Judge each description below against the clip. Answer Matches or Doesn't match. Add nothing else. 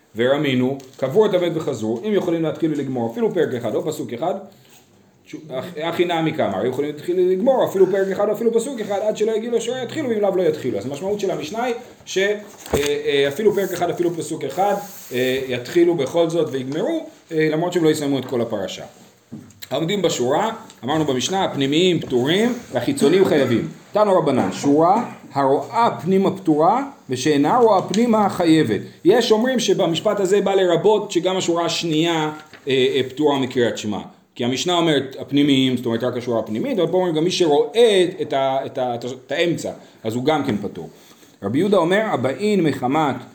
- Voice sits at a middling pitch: Matches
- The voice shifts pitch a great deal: Matches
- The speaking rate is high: Matches